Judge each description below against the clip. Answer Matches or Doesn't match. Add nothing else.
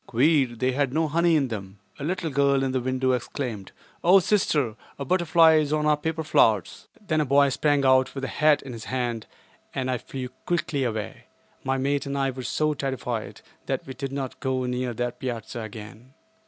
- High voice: Doesn't match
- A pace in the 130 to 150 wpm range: Doesn't match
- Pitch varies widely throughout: Doesn't match